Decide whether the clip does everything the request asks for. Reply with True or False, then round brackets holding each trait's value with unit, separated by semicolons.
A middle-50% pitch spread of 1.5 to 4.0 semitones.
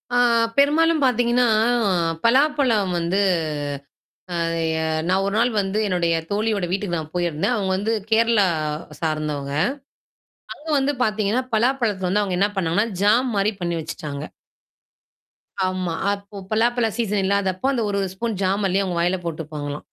False (4.5 semitones)